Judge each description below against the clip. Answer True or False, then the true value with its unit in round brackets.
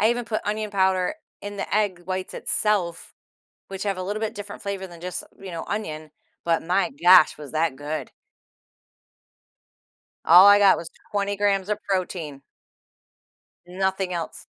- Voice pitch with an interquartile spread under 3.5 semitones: True (2.9 semitones)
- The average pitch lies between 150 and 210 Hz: True (190 Hz)